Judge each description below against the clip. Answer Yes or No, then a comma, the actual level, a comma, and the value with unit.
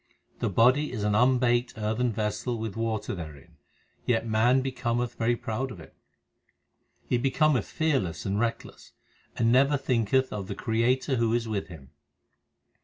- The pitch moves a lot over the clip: No, average, 3.1 semitones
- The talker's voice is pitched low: Yes, low, 115 Hz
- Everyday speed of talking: Yes, average, 150 wpm